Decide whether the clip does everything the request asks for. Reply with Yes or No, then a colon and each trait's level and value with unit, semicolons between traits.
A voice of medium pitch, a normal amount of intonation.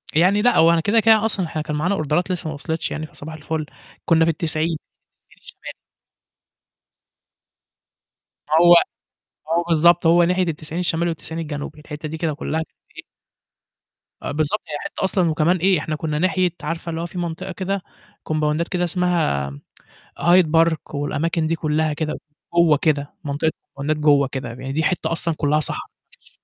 No: medium, 160 Hz; narrow, 2.3 semitones